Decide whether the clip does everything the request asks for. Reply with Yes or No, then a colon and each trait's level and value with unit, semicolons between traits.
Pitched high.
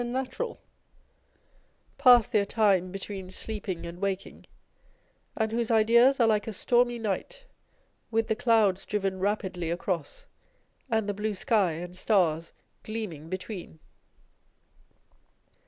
Yes: high, 210 Hz